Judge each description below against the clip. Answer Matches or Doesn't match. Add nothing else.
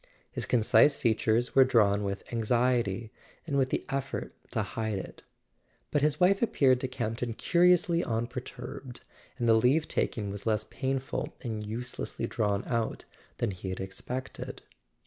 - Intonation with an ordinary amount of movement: Matches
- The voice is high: Doesn't match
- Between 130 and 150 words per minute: Matches